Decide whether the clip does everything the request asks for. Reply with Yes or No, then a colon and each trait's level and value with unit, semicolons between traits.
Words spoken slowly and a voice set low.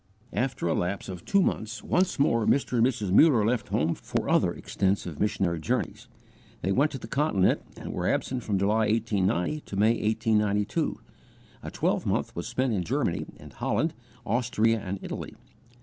No: average, 165 wpm; low, 110 Hz